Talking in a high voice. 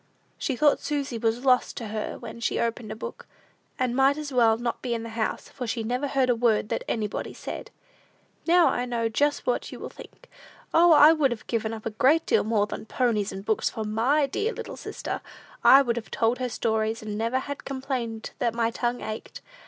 Yes: high, 235 Hz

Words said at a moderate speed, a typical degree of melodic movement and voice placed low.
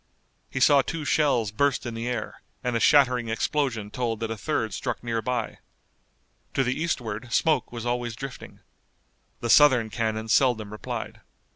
Yes: average, 160 wpm; average, 3.1 semitones; low, 120 Hz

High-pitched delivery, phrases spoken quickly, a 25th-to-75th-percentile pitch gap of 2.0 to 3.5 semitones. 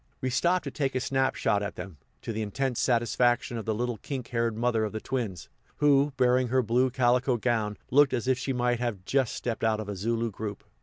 No: low, 120 Hz; fast, 225 wpm; average, 2.9 semitones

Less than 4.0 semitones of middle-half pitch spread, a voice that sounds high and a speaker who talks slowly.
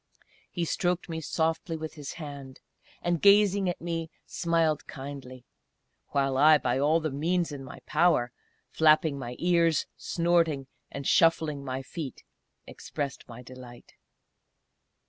No: average, 3.6 semitones; medium, 155 Hz; slow, 130 wpm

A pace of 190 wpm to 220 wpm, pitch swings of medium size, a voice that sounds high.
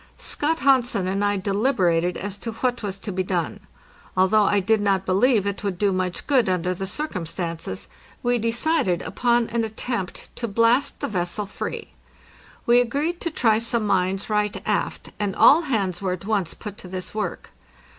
No: average, 175 wpm; average, 4.1 semitones; high, 205 Hz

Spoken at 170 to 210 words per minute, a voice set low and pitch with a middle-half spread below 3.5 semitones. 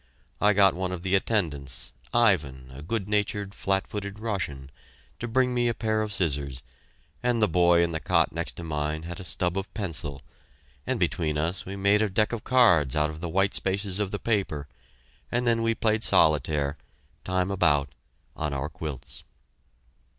No: average, 180 wpm; very low, 95 Hz; wide, 5.4 semitones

